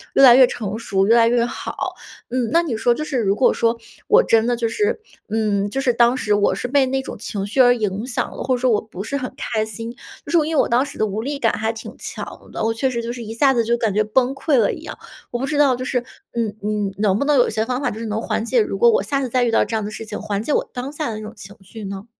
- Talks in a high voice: Yes, high, 235 Hz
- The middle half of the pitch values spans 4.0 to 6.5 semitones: No, average, 3.3 semitones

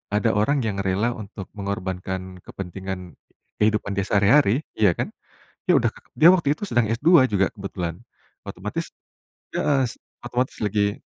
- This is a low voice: Yes, low, 100 Hz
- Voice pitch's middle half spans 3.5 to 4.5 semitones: Yes, average, 3.9 semitones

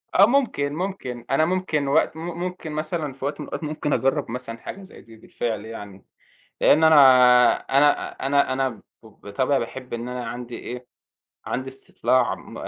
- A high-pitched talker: No, low, 135 Hz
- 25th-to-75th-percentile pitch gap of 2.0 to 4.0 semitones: No, average, 4.4 semitones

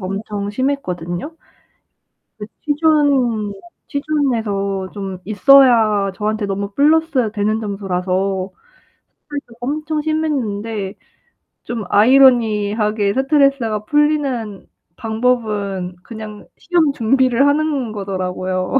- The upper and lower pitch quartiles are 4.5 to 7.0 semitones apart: Yes, wide, 5.5 semitones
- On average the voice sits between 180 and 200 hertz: No, high, 220 Hz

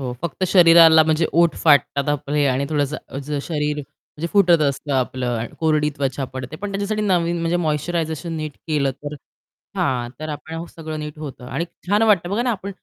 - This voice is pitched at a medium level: Yes, medium, 155 Hz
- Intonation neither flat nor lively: Yes, average, 3.3 semitones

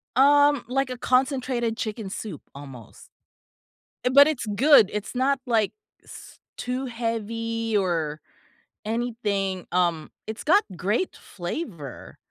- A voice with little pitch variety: No, average, 4.9 semitones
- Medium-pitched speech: No, high, 230 Hz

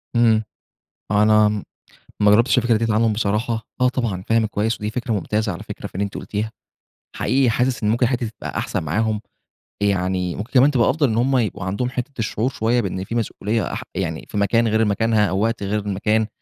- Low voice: Yes, low, 110 Hz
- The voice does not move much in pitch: Yes, narrow, 2.3 semitones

